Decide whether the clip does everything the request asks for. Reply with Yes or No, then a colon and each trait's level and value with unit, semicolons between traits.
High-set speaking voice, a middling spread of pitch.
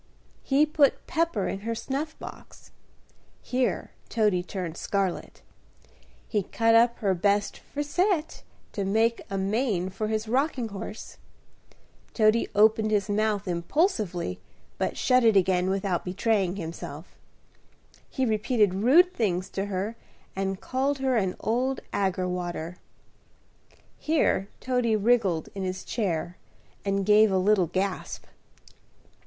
Yes: high, 210 Hz; average, 4.3 semitones